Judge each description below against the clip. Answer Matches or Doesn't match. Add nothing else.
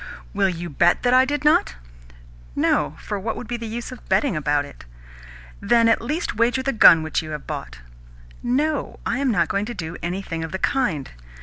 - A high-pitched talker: Matches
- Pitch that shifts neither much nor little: Doesn't match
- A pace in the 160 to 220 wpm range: Matches